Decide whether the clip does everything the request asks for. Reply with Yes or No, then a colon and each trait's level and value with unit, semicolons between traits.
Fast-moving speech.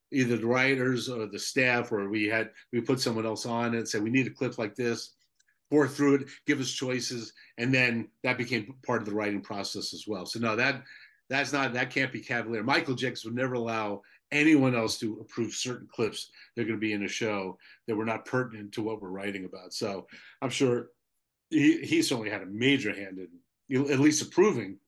Yes: fast, 215 wpm